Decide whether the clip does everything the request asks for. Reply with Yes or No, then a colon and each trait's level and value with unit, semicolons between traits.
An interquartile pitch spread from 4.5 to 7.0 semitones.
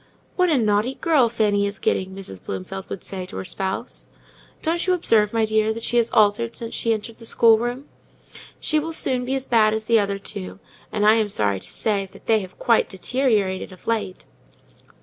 No: average, 3.3 semitones